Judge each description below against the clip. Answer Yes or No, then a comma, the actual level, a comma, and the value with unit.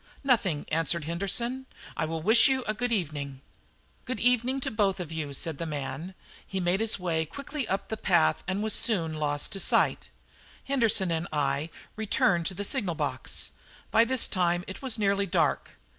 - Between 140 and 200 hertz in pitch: Yes, high, 190 Hz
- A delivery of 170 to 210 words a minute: Yes, average, 175 wpm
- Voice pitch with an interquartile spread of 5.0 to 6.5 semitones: Yes, wide, 5.6 semitones